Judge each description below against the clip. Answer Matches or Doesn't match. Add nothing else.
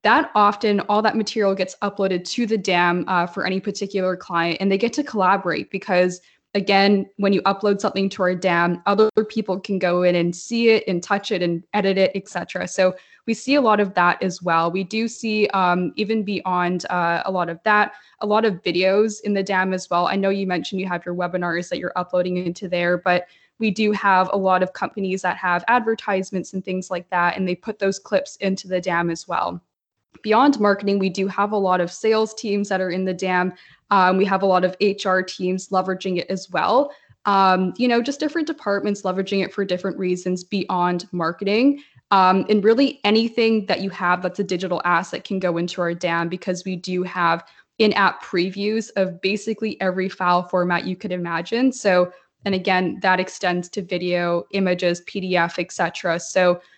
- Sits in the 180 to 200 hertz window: Matches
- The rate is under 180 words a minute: Doesn't match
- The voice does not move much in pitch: Matches